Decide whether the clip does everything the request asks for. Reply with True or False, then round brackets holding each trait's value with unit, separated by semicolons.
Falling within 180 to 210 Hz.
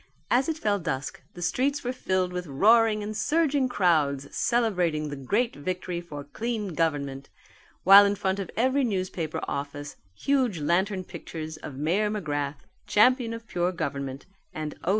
True (185 Hz)